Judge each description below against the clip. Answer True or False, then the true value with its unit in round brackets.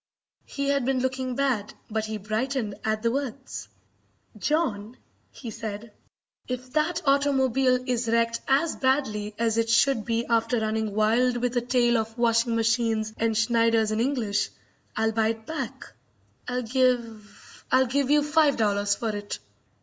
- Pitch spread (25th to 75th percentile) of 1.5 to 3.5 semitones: True (3.0 semitones)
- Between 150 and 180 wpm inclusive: True (155 wpm)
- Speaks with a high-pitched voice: True (235 Hz)